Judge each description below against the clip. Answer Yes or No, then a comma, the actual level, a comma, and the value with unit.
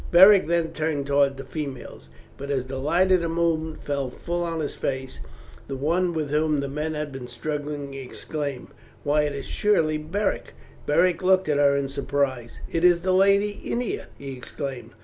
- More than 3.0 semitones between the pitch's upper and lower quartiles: Yes, average, 3.4 semitones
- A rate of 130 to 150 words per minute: No, average, 185 wpm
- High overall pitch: No, medium, 150 Hz